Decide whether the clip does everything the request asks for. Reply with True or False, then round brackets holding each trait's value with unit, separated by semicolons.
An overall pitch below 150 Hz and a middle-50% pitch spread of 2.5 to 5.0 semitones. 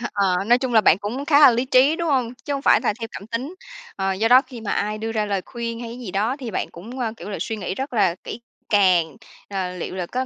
False (225 Hz; 4.2 semitones)